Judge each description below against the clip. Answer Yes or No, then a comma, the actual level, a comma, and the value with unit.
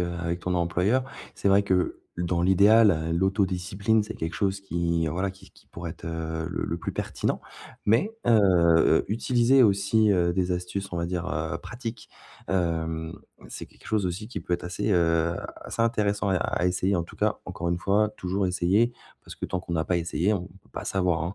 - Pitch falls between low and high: No, very low, 90 Hz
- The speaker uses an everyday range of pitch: Yes, average, 3.0 semitones